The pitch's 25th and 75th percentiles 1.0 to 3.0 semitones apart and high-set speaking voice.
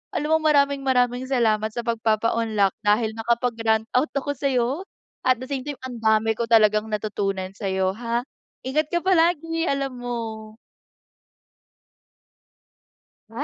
No: average, 3.8 semitones; high, 235 Hz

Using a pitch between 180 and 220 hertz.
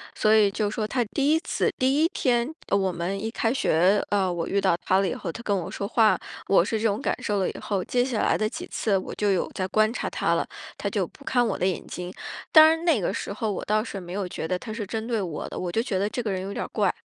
Yes: high, 210 Hz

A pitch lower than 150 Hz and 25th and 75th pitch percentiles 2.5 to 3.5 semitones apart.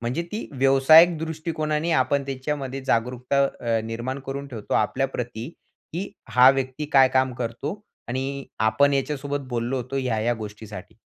Yes: low, 135 Hz; average, 2.9 semitones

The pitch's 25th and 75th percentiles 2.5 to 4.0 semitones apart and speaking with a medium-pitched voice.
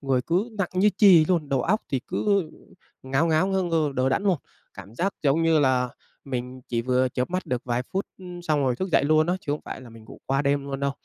No: average, 5.3 semitones; medium, 145 Hz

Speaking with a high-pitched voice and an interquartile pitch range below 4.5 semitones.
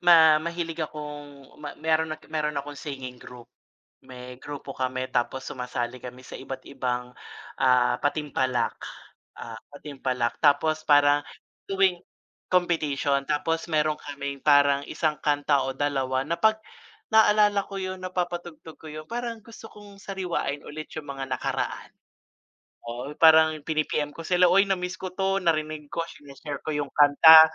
No: medium, 150 Hz; average, 3.5 semitones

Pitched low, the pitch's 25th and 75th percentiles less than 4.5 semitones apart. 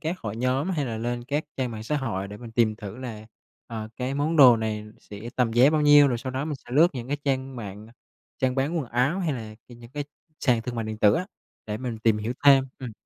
Yes: low, 125 Hz; average, 3.9 semitones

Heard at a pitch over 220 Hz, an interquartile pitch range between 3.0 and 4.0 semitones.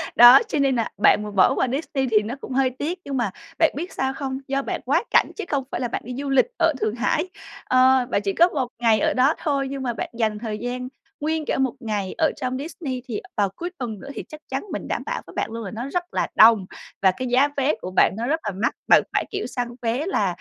Yes: very high, 255 Hz; average, 3.6 semitones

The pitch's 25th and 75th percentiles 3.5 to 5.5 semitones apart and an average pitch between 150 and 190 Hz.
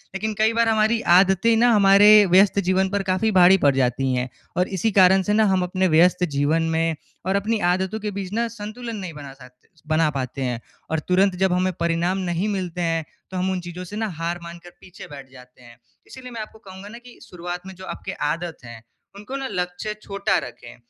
Yes: average, 3.8 semitones; medium, 185 Hz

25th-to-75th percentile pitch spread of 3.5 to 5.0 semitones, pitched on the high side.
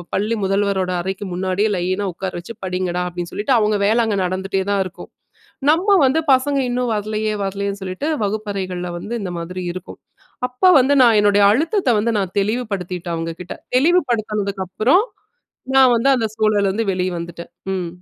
Yes: average, 3.8 semitones; high, 200 Hz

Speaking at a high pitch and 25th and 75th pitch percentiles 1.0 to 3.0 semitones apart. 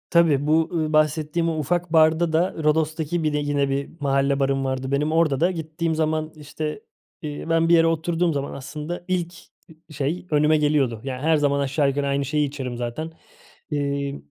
No: medium, 150 Hz; narrow, 2.5 semitones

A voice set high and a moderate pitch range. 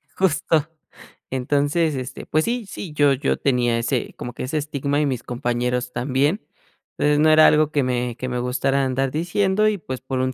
No: medium, 140 Hz; average, 3.7 semitones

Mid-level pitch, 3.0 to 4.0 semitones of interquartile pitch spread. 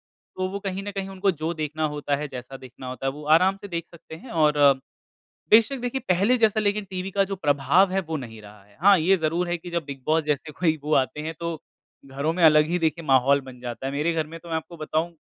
No: medium, 160 Hz; average, 4.4 semitones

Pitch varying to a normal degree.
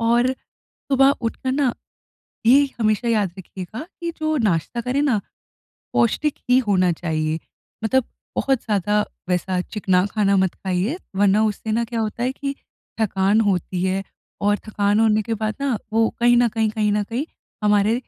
Yes: average, 3.4 semitones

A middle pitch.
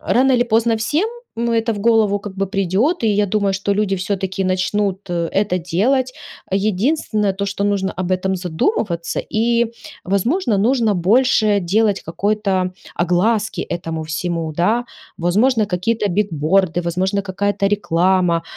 No: high, 200 Hz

